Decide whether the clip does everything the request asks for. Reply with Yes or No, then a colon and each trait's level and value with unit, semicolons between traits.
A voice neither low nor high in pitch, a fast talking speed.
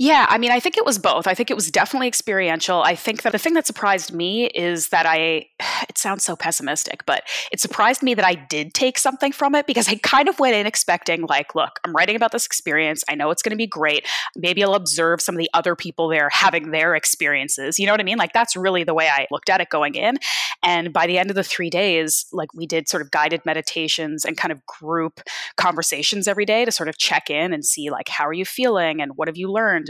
Yes: medium, 180 Hz; fast, 255 wpm